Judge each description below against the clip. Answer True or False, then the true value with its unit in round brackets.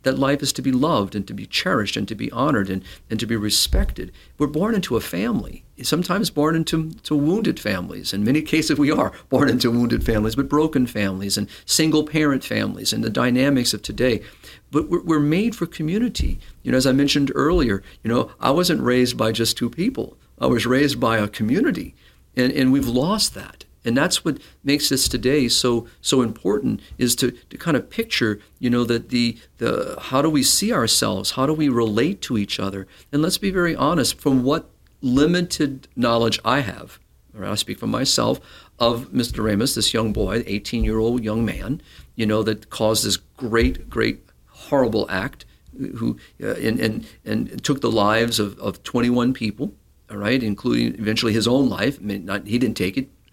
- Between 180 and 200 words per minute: True (195 wpm)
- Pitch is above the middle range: False (120 Hz)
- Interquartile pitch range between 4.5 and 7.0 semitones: True (5.2 semitones)